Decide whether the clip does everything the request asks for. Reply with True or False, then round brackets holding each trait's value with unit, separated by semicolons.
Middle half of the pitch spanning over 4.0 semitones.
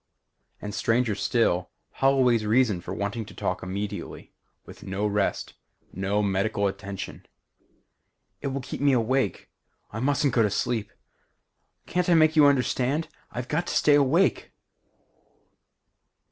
True (5.3 semitones)